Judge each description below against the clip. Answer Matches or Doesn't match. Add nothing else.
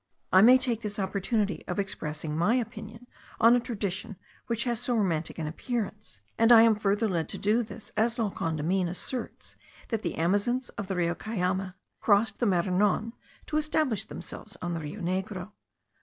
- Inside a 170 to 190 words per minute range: Matches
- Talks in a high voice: Matches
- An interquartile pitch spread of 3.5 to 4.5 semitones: Matches